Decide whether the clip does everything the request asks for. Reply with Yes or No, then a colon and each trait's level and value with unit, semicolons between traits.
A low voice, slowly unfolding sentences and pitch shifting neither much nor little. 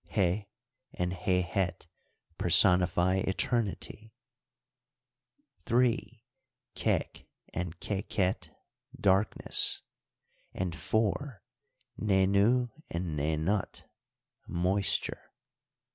Yes: very low, 95 Hz; slow, 60 wpm; average, 3.2 semitones